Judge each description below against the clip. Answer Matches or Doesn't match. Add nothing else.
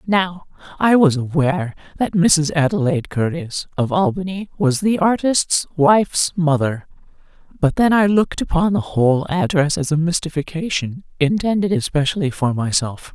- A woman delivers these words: Matches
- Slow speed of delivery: Matches